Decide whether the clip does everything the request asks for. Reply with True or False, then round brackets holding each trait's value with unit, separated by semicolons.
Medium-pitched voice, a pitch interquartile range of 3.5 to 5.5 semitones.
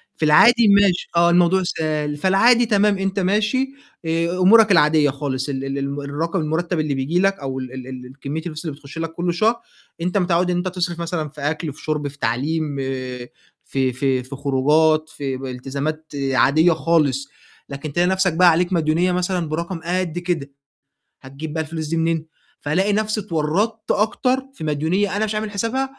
True (160 Hz; 4.3 semitones)